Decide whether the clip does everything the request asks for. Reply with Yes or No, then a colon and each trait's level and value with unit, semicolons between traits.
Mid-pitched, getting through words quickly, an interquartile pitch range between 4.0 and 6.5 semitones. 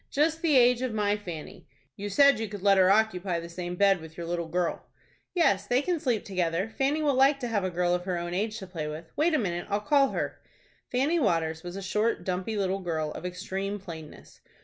No: high, 195 Hz; fast, 225 wpm; wide, 5.5 semitones